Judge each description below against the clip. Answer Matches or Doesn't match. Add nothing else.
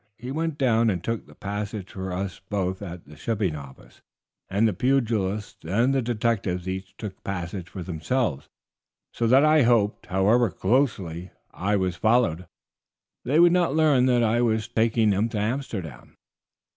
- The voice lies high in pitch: Doesn't match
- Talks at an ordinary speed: Matches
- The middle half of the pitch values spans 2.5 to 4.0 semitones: Doesn't match